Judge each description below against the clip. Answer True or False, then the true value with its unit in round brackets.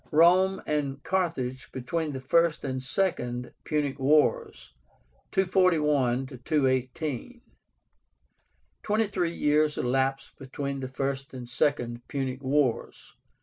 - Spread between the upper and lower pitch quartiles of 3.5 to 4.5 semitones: True (4.0 semitones)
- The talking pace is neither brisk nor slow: False (105 wpm)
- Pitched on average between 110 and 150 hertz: True (140 Hz)